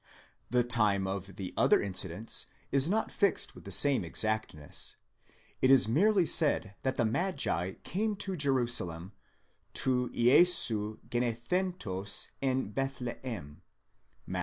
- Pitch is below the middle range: Yes, low, 120 Hz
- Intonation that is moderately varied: No, wide, 5.9 semitones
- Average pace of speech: No, slow, 120 wpm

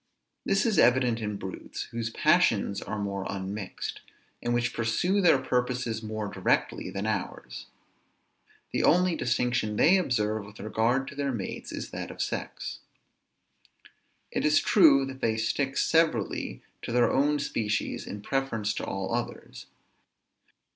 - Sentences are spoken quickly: No, average, 140 wpm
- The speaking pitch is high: No, low, 120 Hz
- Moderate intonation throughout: Yes, average, 4.4 semitones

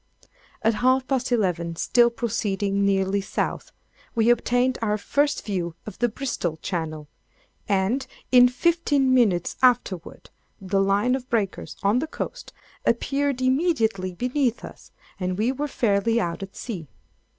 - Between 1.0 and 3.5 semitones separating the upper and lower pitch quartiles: No, average, 4.7 semitones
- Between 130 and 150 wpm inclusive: Yes, average, 140 wpm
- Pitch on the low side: No, high, 225 Hz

